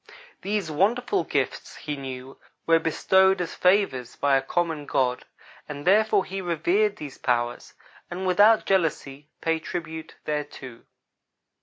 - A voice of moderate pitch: Yes, medium, 165 Hz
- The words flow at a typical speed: No, slow, 130 wpm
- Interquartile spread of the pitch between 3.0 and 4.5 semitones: No, average, 5.1 semitones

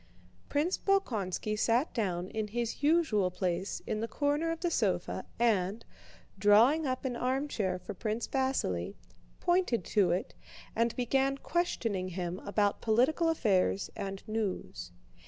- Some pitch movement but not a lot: No, wide, 6.0 semitones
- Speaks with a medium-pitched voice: No, high, 225 Hz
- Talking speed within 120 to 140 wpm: Yes, slow, 135 wpm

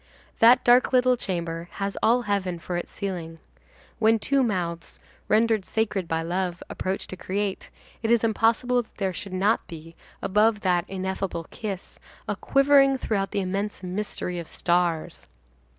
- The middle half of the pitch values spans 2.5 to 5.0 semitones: Yes, average, 4.1 semitones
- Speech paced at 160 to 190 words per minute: No, average, 150 wpm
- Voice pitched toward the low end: No, high, 195 Hz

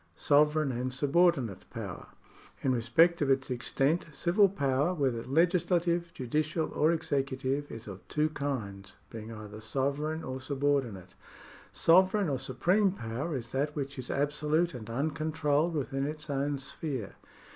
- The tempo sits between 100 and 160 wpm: Yes, average, 140 wpm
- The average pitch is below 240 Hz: Yes, medium, 140 Hz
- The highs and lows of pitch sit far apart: No, average, 3.5 semitones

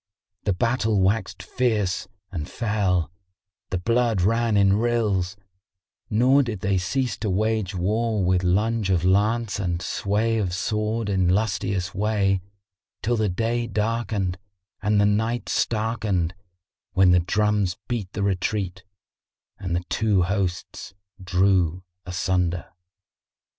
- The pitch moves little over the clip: No, average, 3.3 semitones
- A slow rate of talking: Yes, slow, 125 wpm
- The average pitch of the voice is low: Yes, low, 100 Hz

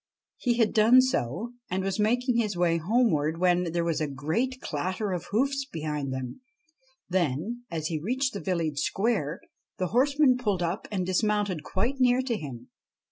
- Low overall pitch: No, high, 190 Hz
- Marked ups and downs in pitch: Yes, wide, 6.8 semitones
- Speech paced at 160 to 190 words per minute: Yes, average, 170 wpm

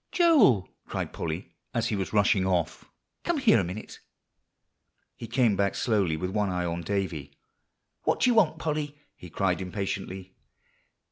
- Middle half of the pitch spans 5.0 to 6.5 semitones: Yes, wide, 5.5 semitones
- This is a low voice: Yes, low, 100 Hz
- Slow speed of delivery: No, average, 155 wpm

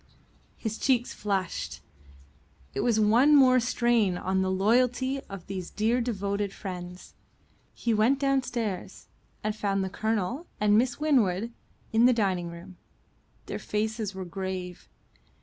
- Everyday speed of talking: No, slow, 130 wpm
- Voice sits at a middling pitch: No, high, 210 Hz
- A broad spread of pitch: No, average, 4.2 semitones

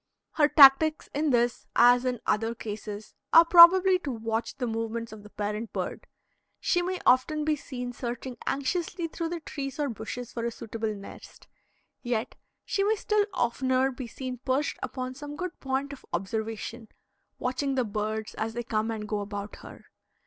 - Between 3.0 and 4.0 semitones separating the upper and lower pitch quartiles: No, average, 4.6 semitones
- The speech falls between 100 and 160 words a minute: No, average, 170 wpm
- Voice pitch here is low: No, very high, 250 Hz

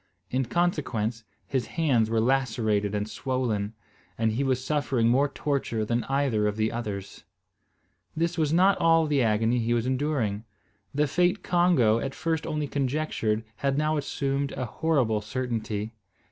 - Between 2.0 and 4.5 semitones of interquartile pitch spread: No, average, 4.9 semitones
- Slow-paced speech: No, average, 150 wpm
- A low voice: Yes, low, 130 Hz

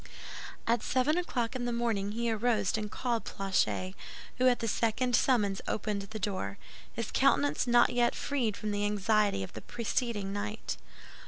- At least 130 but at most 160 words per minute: No, average, 170 wpm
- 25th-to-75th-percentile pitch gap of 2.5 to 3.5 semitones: Yes, average, 3.2 semitones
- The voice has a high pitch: Yes, high, 220 Hz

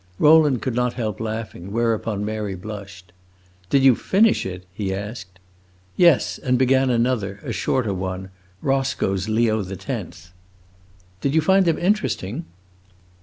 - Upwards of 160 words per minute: No, slow, 135 wpm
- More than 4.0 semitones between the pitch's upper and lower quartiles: Yes, wide, 5.5 semitones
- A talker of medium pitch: No, low, 110 Hz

